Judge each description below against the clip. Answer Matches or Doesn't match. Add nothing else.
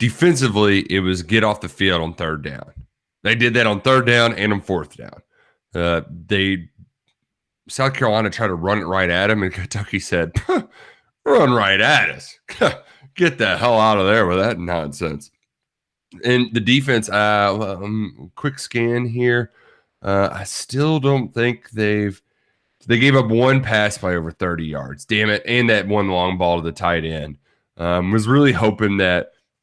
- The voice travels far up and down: Doesn't match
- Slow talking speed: Doesn't match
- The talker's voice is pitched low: Matches